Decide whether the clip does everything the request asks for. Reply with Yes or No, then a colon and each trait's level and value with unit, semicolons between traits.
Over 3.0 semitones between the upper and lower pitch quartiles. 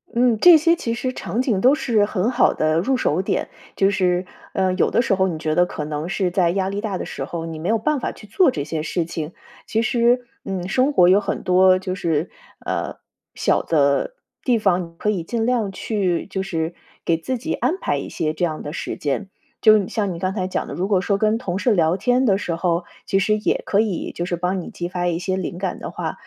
Yes: average, 4.2 semitones